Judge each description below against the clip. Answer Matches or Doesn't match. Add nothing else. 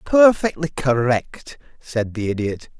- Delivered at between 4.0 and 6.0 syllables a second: Doesn't match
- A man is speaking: Matches